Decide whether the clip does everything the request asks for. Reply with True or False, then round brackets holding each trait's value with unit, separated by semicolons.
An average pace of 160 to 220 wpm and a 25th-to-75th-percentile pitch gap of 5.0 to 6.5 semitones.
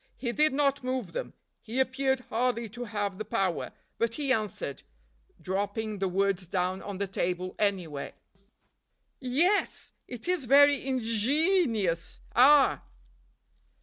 False (135 wpm; 5.4 semitones)